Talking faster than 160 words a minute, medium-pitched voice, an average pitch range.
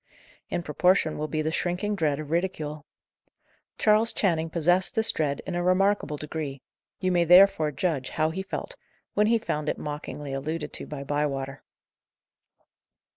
No: average, 155 wpm; medium, 160 Hz; average, 3.7 semitones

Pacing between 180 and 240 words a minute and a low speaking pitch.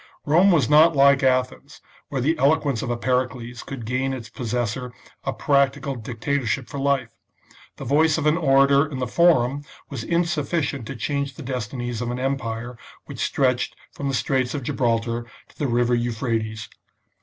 No: average, 165 wpm; low, 130 Hz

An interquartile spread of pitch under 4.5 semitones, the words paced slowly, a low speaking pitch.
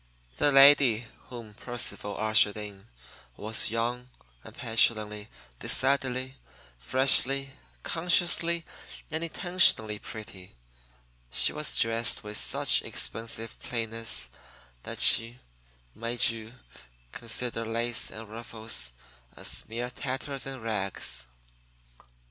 Yes: average, 3.3 semitones; slow, 95 wpm; low, 115 Hz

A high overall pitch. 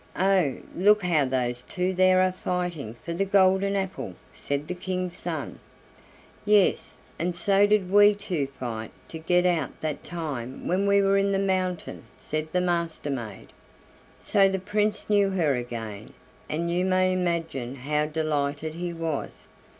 No: medium, 175 Hz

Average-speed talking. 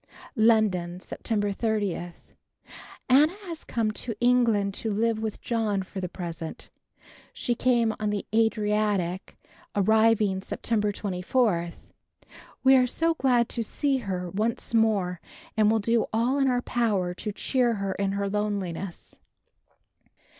No: slow, 130 wpm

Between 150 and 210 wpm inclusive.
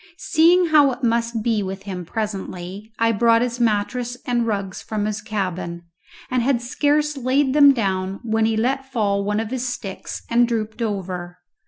Yes: average, 175 wpm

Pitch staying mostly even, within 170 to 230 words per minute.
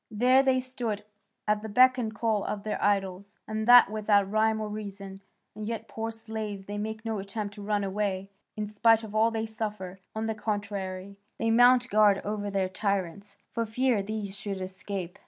Yes: narrow, 1.8 semitones; average, 190 wpm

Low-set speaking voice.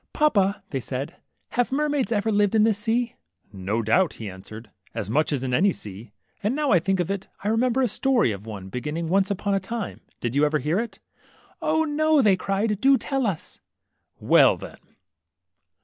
No: high, 195 Hz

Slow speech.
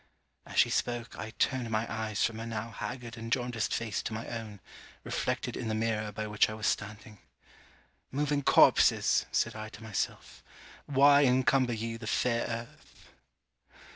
No: average, 165 wpm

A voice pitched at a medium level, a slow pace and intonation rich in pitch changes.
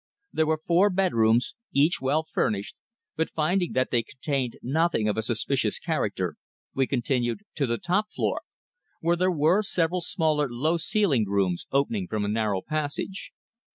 No: medium, 150 Hz; average, 155 wpm; wide, 6.5 semitones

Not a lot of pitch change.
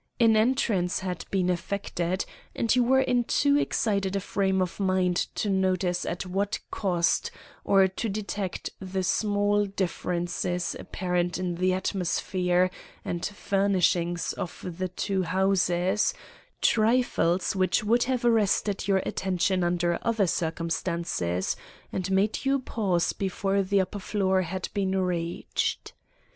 Yes: narrow, 2.3 semitones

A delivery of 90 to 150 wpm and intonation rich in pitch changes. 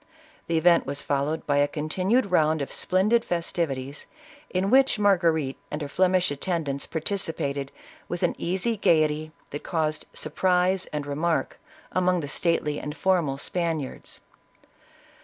No: slow, 135 wpm; average, 3.8 semitones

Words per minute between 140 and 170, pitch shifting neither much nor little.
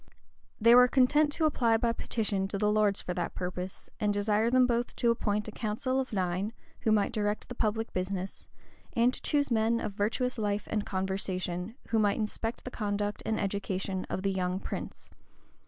No: average, 190 wpm; average, 3.1 semitones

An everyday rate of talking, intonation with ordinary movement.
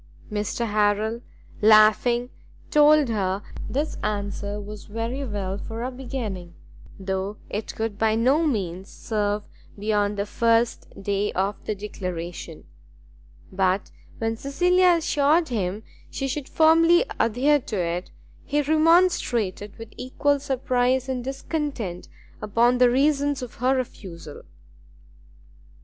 No: slow, 120 wpm; average, 4.9 semitones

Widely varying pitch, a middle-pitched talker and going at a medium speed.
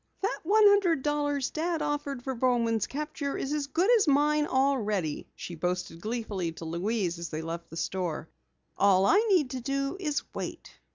No: wide, 8.2 semitones; very high, 260 Hz; average, 175 wpm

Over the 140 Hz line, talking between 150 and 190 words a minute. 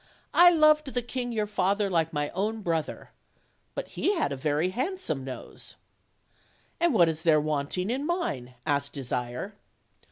Yes: medium, 185 Hz; average, 155 wpm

